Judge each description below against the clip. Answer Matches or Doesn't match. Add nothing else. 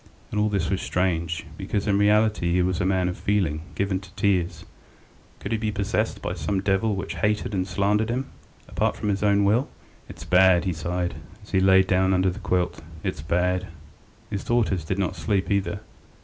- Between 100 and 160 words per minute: Doesn't match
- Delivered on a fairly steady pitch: Matches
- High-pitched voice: Doesn't match